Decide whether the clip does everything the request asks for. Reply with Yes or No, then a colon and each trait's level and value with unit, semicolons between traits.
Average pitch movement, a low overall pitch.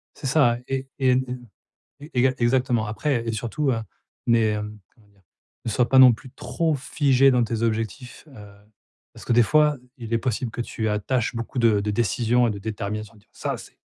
Yes: average, 3.1 semitones; low, 120 Hz